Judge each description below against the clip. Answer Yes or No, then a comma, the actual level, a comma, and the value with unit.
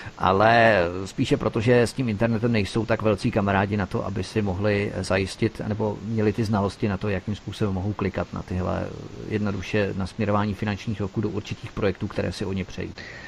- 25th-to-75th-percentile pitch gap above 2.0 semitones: Yes, narrow, 2.4 semitones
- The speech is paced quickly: Yes, fast, 185 wpm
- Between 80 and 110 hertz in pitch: Yes, low, 105 Hz